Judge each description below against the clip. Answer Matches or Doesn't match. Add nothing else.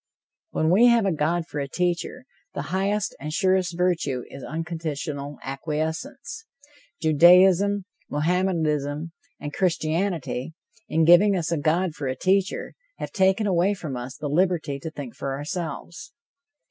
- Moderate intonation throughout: Matches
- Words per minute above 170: Doesn't match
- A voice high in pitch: Doesn't match